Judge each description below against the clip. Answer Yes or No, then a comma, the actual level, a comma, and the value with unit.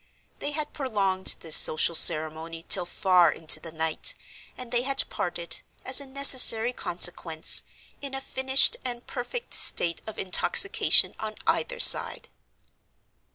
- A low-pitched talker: No, high, 220 Hz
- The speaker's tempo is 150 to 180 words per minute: No, slow, 135 wpm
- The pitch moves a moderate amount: No, wide, 7.8 semitones